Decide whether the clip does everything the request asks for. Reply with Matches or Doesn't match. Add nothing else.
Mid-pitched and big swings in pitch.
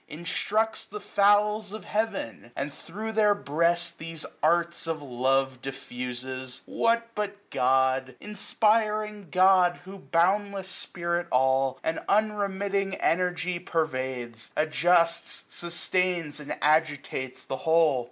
Matches